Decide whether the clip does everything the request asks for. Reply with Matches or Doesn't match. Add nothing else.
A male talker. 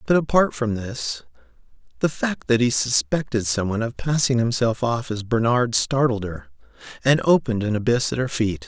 Matches